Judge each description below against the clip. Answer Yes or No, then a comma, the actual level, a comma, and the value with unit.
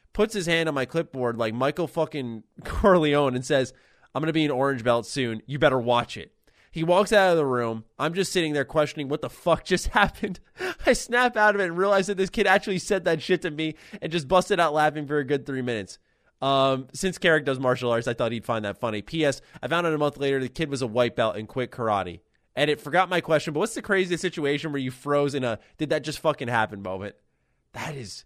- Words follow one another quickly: Yes, fast, 250 wpm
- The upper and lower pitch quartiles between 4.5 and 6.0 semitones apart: Yes, wide, 5.5 semitones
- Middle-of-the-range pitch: Yes, medium, 145 Hz